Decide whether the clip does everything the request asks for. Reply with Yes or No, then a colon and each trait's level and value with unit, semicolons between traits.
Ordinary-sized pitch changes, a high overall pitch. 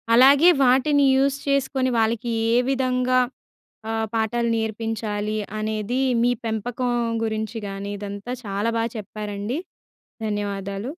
Yes: average, 3.2 semitones; high, 225 Hz